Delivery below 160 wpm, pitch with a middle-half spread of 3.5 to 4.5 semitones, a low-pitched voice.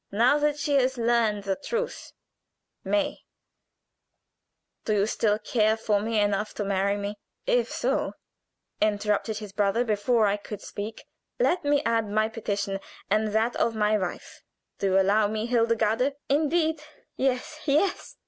No: average, 150 wpm; average, 4.0 semitones; high, 220 Hz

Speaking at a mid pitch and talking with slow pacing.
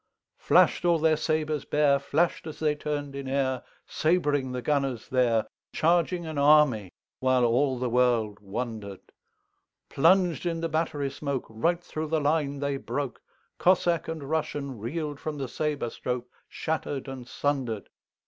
Yes: medium, 145 Hz; slow, 120 wpm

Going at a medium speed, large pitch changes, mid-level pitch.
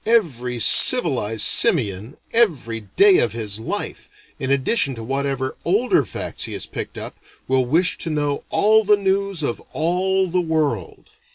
Yes: average, 155 wpm; wide, 7.7 semitones; medium, 155 Hz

